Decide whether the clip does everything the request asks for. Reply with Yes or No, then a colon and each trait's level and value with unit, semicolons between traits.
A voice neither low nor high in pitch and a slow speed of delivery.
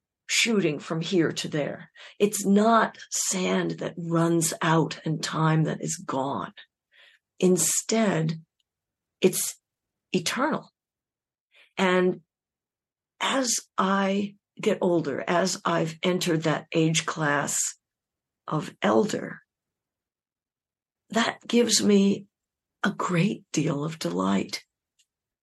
Yes: medium, 175 Hz; slow, 95 wpm